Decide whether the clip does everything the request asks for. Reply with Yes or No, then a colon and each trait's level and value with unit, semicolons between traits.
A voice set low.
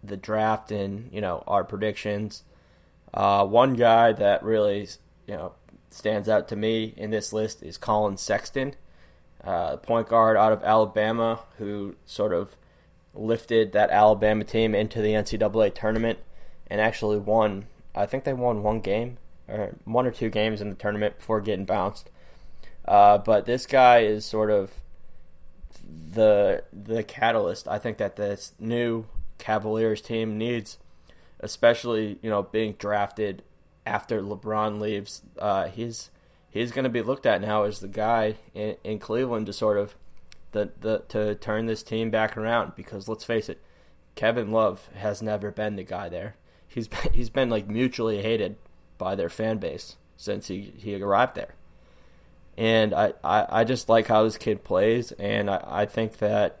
Yes: low, 110 Hz